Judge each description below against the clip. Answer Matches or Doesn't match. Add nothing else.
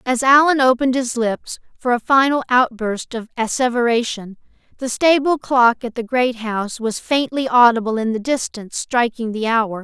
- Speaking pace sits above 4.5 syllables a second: Matches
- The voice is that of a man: Doesn't match